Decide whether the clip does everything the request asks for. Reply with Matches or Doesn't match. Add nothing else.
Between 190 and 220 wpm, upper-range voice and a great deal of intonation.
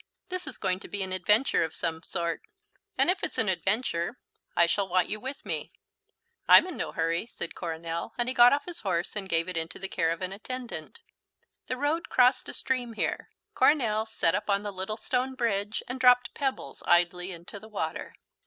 Matches